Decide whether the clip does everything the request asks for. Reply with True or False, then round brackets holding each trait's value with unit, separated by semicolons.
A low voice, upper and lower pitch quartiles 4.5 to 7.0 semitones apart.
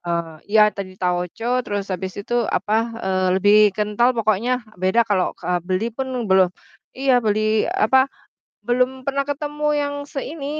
False (210 Hz; 5.2 semitones)